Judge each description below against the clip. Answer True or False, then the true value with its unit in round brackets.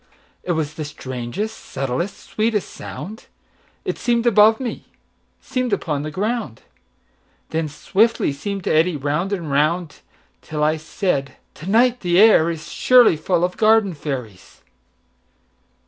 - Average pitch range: False (6.3 semitones)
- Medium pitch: True (175 Hz)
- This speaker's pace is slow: True (120 wpm)